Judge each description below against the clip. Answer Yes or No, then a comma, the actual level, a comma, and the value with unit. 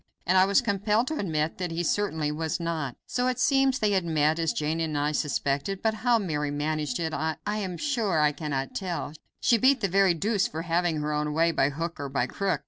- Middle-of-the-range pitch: Yes, medium, 165 Hz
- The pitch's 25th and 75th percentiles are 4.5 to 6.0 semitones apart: Yes, average, 4.9 semitones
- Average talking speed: No, fast, 225 wpm